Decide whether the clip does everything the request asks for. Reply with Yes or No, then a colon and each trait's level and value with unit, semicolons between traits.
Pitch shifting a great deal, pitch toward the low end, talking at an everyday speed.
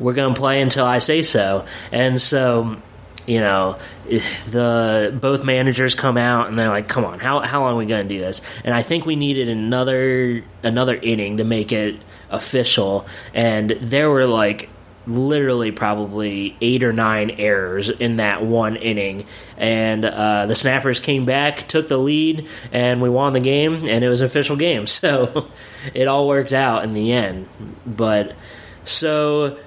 No: average, 3.8 semitones; low, 120 Hz; average, 175 wpm